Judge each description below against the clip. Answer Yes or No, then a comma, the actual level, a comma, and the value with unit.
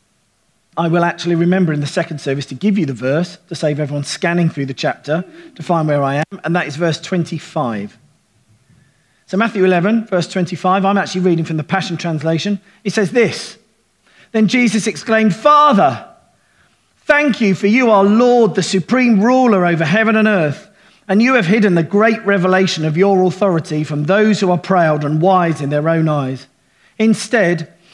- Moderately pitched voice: Yes, medium, 180 Hz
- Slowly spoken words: No, average, 180 wpm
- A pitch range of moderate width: Yes, average, 4.9 semitones